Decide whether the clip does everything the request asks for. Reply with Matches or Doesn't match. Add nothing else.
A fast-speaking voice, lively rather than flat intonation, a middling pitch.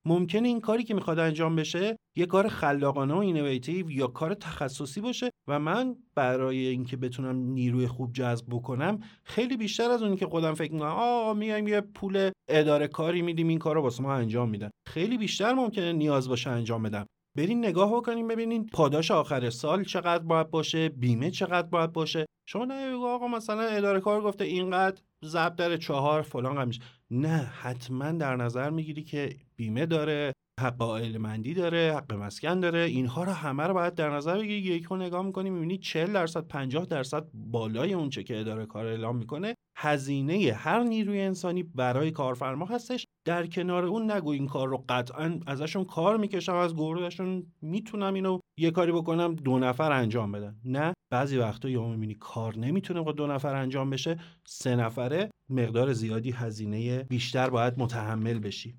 Matches